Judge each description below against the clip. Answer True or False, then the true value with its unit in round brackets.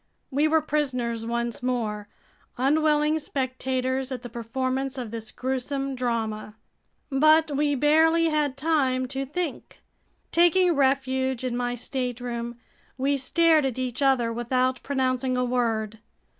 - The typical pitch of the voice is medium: False (260 Hz)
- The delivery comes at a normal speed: False (130 wpm)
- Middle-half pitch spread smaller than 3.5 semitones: True (2.8 semitones)